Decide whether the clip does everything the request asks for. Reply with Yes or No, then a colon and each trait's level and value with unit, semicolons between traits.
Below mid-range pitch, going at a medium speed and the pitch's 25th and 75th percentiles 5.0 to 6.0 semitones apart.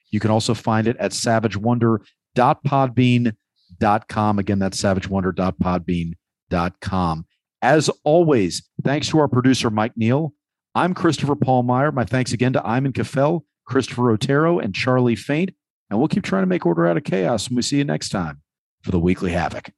Yes: low, 120 Hz; average, 165 wpm; wide, 5.5 semitones